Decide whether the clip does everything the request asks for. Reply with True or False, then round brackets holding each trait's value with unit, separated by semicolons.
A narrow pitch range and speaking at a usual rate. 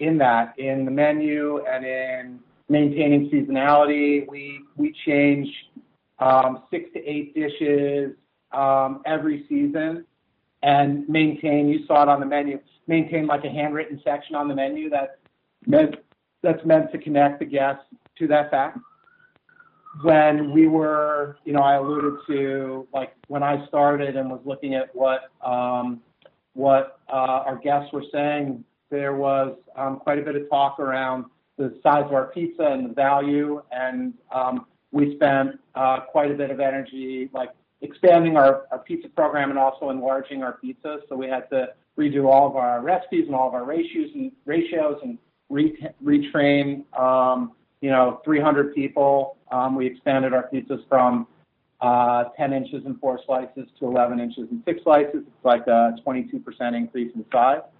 True (2.3 semitones; 165 wpm)